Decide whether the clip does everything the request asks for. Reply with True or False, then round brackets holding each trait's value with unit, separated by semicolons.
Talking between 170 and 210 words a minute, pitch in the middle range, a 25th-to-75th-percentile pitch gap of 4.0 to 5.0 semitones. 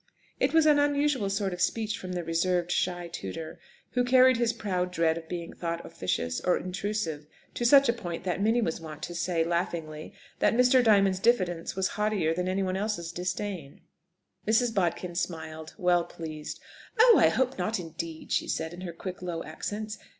True (180 wpm; 180 Hz; 4.5 semitones)